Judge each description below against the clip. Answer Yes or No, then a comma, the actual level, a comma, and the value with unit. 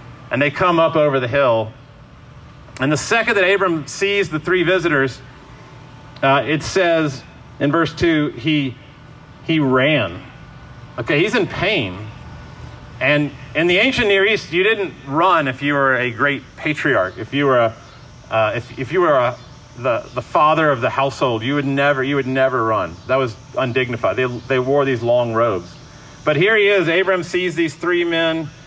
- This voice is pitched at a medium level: Yes, medium, 145 Hz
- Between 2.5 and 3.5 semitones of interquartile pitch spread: No, average, 3.9 semitones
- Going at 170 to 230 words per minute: Yes, average, 180 wpm